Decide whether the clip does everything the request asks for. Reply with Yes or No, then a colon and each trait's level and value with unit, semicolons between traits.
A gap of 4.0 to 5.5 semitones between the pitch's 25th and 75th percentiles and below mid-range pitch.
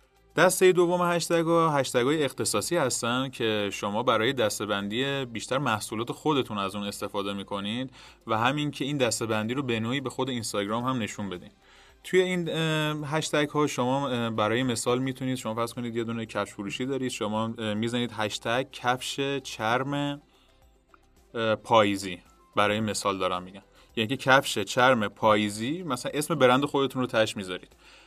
Yes: average, 4.5 semitones; low, 120 Hz